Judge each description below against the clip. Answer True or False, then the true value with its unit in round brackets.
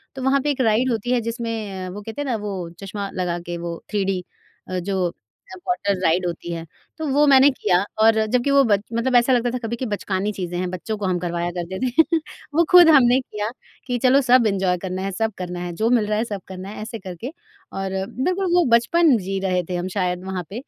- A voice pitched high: True (210 Hz)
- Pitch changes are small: False (5.1 semitones)